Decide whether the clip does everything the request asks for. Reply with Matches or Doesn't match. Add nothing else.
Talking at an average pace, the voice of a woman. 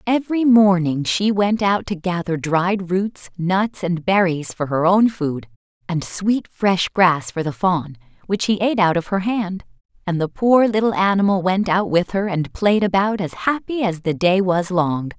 Matches